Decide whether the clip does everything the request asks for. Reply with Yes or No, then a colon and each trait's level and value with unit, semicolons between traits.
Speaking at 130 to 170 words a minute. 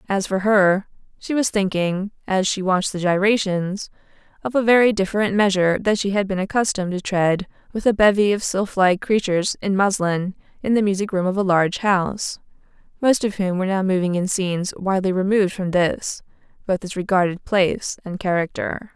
No: average, 185 wpm